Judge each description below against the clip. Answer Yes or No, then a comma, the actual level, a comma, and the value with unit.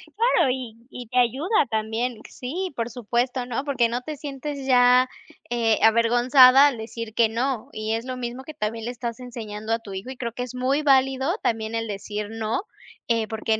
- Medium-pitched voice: No, high, 245 Hz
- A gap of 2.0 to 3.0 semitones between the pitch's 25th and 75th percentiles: Yes, narrow, 2.6 semitones